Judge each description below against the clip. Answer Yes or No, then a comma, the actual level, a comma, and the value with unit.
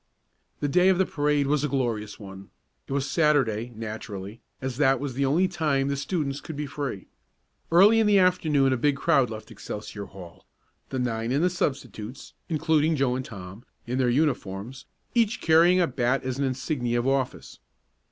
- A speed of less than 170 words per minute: No, average, 180 wpm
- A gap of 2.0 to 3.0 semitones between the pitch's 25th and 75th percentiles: No, average, 4.3 semitones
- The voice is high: No, low, 135 Hz